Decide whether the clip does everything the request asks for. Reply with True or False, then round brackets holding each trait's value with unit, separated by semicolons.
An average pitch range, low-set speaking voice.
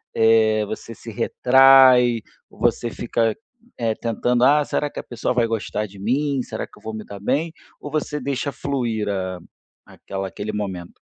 True (3.7 semitones; 115 Hz)